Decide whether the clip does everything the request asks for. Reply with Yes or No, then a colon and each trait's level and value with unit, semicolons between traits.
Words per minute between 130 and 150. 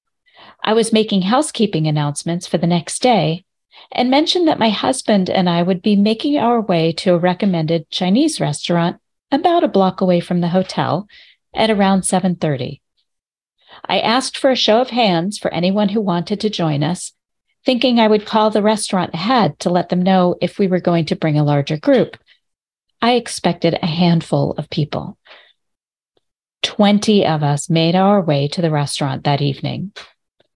No: average, 170 wpm